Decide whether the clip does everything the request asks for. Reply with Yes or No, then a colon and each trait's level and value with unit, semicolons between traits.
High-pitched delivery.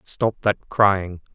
No: low, 100 Hz